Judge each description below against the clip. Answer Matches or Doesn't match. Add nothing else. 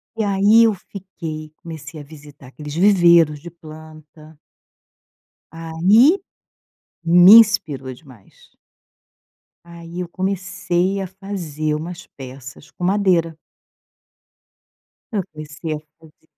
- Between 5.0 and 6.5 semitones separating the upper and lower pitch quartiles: Doesn't match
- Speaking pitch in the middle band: Matches